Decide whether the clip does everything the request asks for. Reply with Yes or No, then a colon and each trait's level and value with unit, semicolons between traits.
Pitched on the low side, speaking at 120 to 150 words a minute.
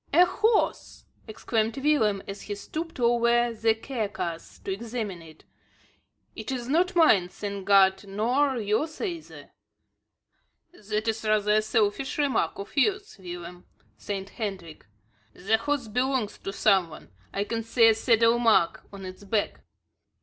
No: high, 220 Hz; average, 140 wpm